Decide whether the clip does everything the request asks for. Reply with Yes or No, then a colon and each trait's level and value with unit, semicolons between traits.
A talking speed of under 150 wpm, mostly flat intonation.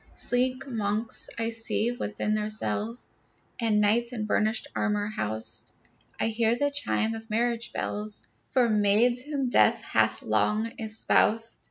Yes: average, 140 wpm; narrow, 2.1 semitones